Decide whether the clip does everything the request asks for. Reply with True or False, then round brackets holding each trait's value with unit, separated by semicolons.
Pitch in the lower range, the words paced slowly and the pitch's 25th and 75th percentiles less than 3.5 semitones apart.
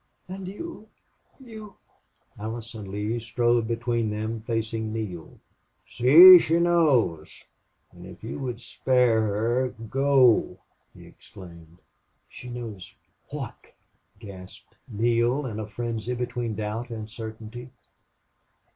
True (115 Hz; 110 wpm; 2.7 semitones)